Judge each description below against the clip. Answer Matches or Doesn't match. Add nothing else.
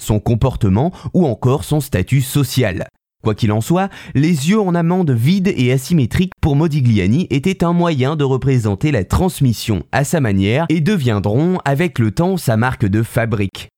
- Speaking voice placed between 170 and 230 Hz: Doesn't match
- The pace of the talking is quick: Doesn't match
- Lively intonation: Matches